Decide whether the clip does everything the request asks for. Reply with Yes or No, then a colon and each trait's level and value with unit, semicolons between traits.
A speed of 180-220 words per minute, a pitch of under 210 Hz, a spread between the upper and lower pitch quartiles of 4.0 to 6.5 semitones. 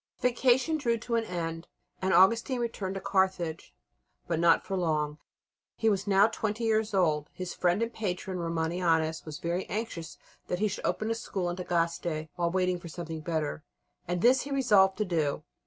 Yes: average, 185 wpm; medium, 185 Hz; average, 4.6 semitones